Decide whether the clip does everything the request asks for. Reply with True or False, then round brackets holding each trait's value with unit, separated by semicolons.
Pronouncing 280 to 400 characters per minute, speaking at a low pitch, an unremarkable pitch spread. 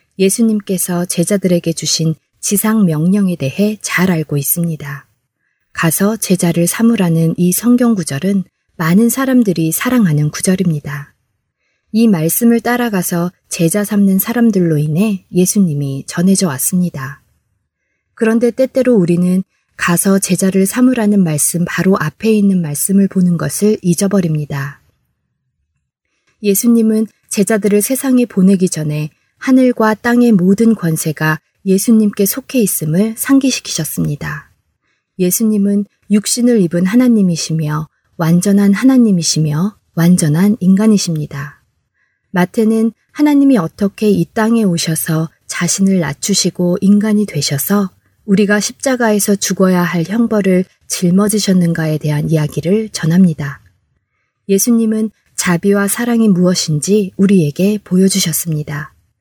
False (290 characters per minute; 190 Hz; 4.5 semitones)